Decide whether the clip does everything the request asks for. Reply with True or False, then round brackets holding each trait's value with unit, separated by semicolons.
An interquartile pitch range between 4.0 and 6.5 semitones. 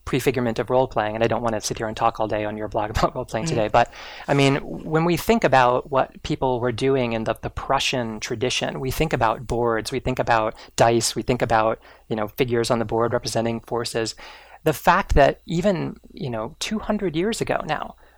False (3.2 semitones)